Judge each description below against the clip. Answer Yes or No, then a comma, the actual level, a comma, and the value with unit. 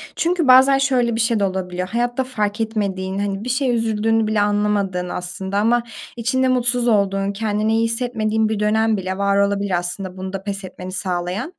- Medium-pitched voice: No, high, 210 Hz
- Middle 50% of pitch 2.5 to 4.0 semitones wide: Yes, average, 3.2 semitones